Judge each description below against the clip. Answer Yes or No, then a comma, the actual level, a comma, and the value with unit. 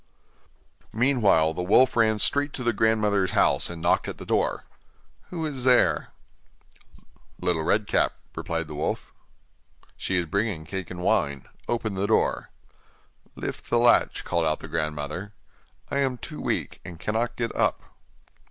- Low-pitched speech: Yes, low, 100 Hz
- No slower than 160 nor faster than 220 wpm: No, average, 150 wpm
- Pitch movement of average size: No, wide, 6.2 semitones